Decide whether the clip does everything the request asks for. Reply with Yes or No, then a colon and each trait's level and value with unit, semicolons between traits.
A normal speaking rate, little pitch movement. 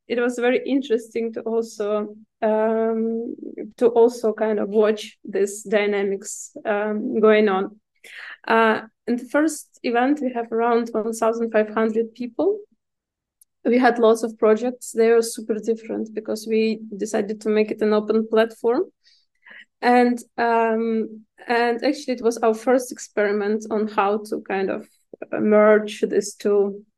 Yes: average, 145 wpm; narrow, 1.7 semitones